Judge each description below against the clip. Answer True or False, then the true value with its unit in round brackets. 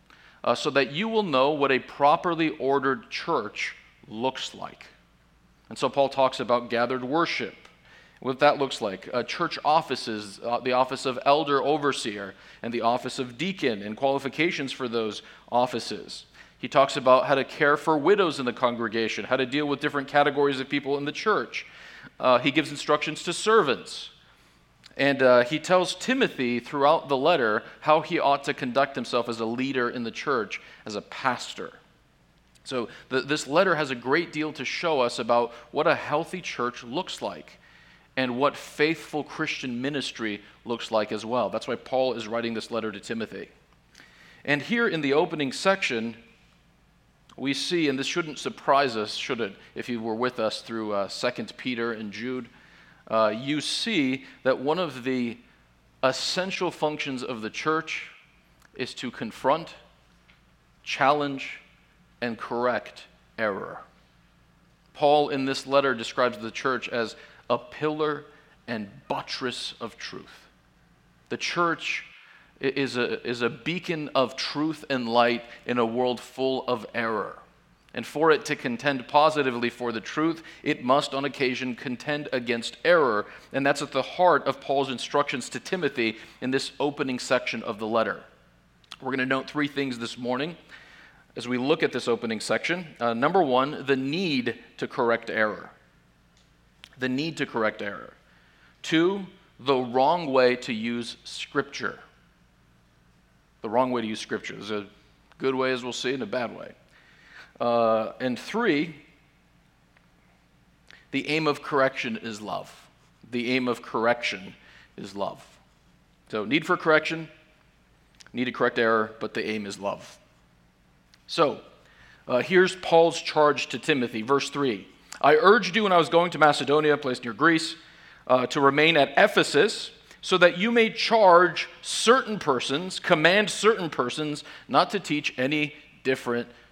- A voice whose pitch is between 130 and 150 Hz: True (135 Hz)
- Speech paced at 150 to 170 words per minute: True (160 wpm)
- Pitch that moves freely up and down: False (4.0 semitones)